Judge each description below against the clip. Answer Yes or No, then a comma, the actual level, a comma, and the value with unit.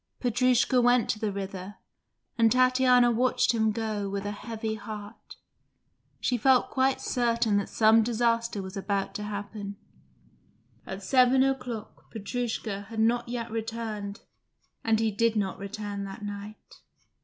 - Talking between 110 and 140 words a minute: Yes, slow, 135 wpm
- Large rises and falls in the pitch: No, average, 2.9 semitones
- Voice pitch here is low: No, high, 220 Hz